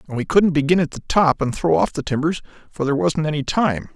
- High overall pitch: No, medium, 150 Hz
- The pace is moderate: No, fast, 260 wpm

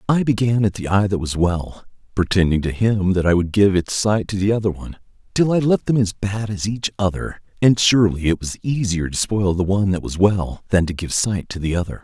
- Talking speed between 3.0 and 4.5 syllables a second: No, 5.5 syllables/s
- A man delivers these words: Yes, male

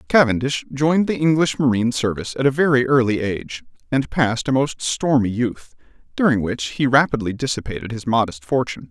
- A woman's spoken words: No, male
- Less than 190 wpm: Yes, average, 170 wpm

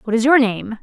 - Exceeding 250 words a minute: Yes, fast, 290 wpm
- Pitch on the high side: Yes, high, 235 Hz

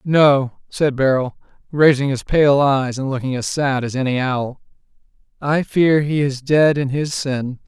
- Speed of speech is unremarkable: Yes, average, 170 wpm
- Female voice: No, male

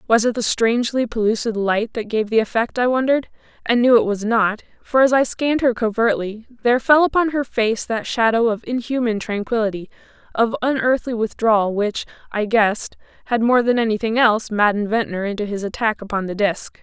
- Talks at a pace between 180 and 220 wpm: Yes, average, 185 wpm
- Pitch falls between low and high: No, high, 225 Hz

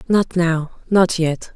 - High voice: No, medium, 175 Hz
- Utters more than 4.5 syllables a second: No, 3.1 syllables/s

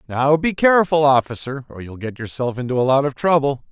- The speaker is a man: Yes, male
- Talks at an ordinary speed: No, fast, 210 wpm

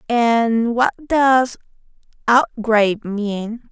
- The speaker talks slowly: Yes, slow, 80 wpm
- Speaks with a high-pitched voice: Yes, high, 230 Hz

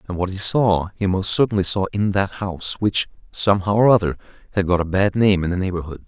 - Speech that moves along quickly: Yes, fast, 225 wpm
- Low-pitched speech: Yes, very low, 95 Hz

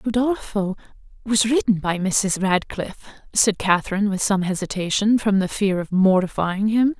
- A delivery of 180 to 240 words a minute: No, average, 145 wpm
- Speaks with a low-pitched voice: No, high, 200 Hz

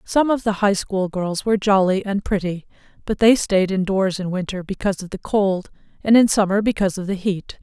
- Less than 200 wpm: No, fast, 205 wpm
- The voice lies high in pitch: Yes, high, 195 Hz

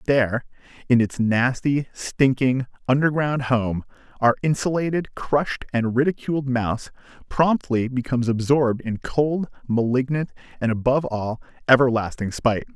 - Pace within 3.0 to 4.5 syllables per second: No, 4.8 syllables/s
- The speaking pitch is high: No, low, 130 Hz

